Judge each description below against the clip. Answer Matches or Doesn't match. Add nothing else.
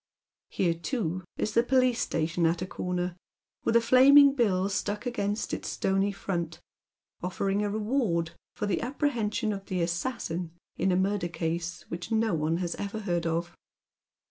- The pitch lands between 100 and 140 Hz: Doesn't match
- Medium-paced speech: Matches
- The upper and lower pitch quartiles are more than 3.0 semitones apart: Matches